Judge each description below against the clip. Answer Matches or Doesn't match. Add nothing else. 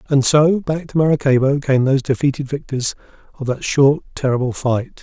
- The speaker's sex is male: Matches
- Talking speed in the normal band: Matches